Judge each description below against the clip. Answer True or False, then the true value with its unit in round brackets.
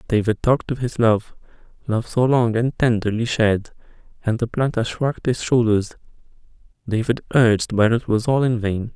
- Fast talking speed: False (160 wpm)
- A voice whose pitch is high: False (115 Hz)